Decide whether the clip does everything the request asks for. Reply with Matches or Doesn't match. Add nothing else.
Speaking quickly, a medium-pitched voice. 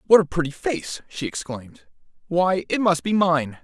Doesn't match